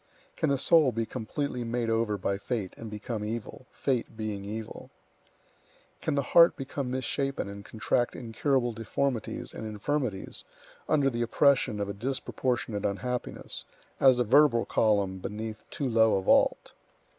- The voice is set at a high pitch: No, low, 115 Hz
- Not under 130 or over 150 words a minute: Yes, average, 145 wpm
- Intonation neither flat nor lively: Yes, average, 3.8 semitones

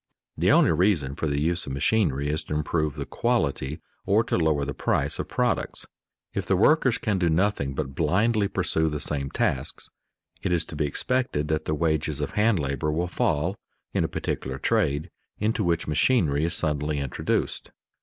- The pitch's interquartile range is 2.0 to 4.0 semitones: No, average, 4.7 semitones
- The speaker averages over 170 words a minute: Yes, average, 185 wpm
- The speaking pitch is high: No, very low, 80 Hz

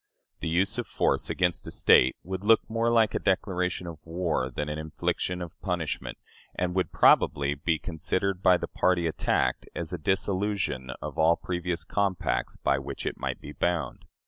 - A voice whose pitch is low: Yes, very low, 90 Hz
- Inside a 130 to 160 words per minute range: No, average, 175 wpm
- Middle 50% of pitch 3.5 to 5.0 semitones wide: No, average, 3.0 semitones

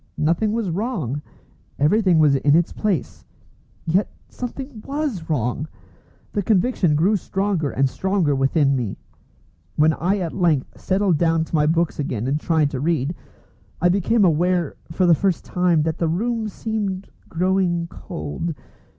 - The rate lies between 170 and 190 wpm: No, average, 150 wpm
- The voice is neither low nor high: Yes, medium, 170 Hz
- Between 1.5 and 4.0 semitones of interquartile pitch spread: No, average, 4.6 semitones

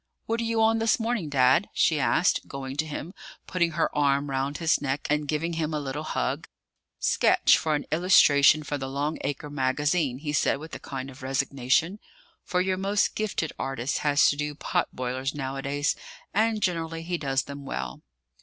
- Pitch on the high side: No, medium, 150 Hz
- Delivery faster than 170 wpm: Yes, average, 185 wpm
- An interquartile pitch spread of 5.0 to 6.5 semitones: No, average, 3.5 semitones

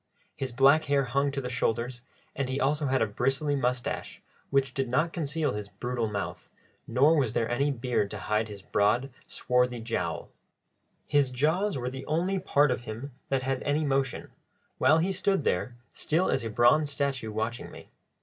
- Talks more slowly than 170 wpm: No, average, 180 wpm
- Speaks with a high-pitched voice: No, low, 135 Hz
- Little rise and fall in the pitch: No, average, 3.2 semitones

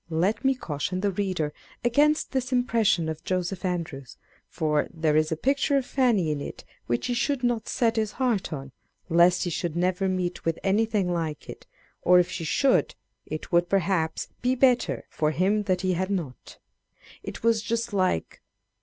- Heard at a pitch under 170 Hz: No, medium, 185 Hz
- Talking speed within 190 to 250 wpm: No, average, 180 wpm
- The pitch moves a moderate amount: No, wide, 5.8 semitones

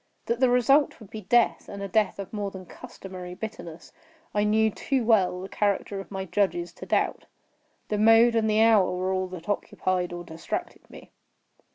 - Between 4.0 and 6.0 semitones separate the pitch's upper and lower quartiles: No, average, 3.1 semitones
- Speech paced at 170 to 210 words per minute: Yes, average, 190 wpm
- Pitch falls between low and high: No, high, 200 Hz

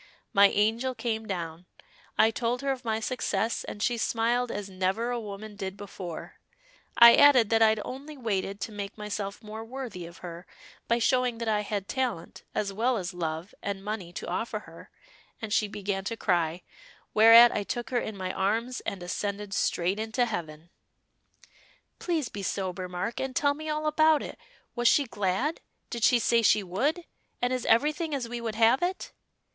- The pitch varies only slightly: No, average, 3.7 semitones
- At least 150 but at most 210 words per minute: Yes, average, 185 wpm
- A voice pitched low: No, high, 220 Hz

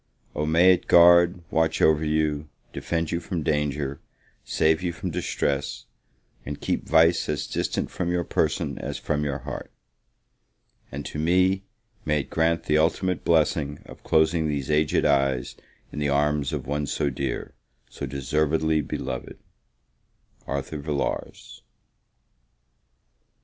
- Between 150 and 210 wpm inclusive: No, slow, 135 wpm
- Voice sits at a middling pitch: No, very low, 75 Hz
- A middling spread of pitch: No, narrow, 2.3 semitones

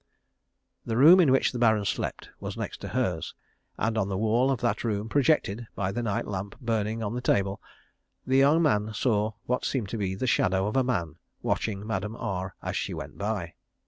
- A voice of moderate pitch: No, low, 110 Hz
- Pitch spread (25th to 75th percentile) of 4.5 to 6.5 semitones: No, average, 3.7 semitones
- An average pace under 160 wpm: No, fast, 205 wpm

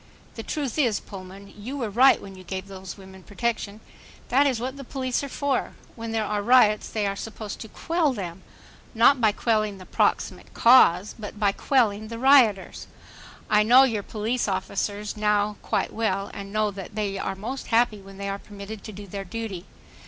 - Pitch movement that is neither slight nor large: Yes, average, 3.0 semitones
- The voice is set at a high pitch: Yes, high, 210 Hz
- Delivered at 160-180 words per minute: No, average, 190 wpm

